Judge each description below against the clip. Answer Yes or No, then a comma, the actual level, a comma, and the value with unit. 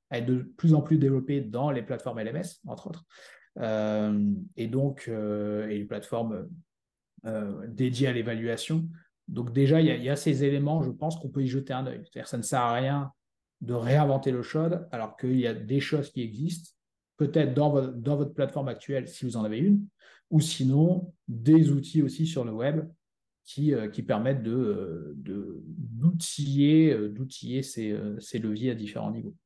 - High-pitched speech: No, low, 135 Hz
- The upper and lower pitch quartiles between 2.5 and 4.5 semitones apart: No, average, 4.9 semitones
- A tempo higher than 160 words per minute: Yes, average, 190 wpm